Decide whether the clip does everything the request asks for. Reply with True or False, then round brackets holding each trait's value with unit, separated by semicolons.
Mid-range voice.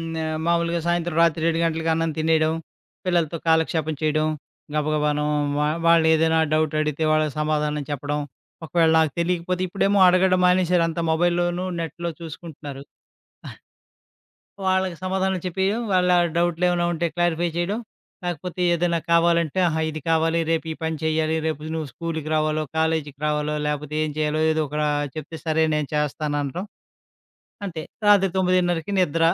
True (160 Hz)